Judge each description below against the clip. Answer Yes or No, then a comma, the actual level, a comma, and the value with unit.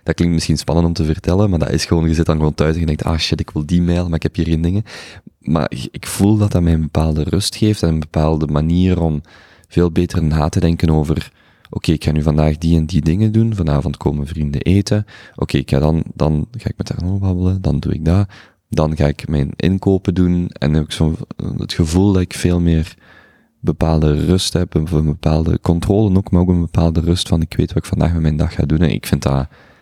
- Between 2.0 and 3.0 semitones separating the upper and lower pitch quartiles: Yes, average, 2.7 semitones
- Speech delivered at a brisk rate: Yes, fast, 255 wpm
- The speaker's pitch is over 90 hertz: No, very low, 85 Hz